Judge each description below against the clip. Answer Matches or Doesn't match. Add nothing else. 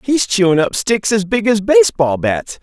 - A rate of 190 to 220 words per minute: Matches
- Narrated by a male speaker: Matches